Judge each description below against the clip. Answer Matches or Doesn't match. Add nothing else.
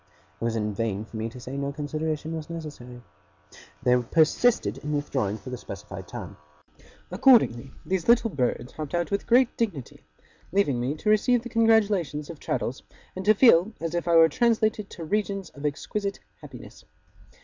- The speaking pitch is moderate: Matches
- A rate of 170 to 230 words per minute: Matches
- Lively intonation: Matches